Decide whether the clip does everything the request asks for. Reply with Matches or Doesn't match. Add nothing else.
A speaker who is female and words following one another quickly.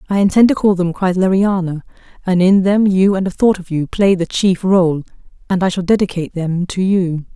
Matches